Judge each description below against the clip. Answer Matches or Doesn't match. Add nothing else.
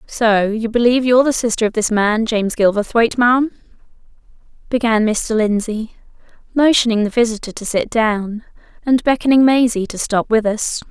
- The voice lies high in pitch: Matches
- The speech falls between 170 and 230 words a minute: Doesn't match